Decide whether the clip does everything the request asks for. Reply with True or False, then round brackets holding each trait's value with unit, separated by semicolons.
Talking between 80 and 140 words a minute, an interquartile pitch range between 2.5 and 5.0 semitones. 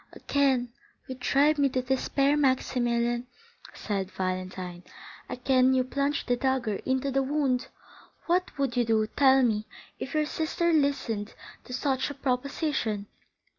True (135 wpm; 2.9 semitones)